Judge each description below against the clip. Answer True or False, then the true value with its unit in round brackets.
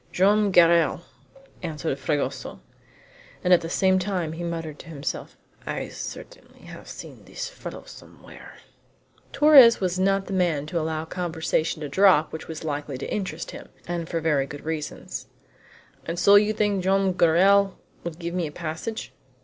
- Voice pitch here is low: False (170 Hz)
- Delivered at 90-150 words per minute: False (165 wpm)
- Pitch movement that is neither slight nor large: True (3.3 semitones)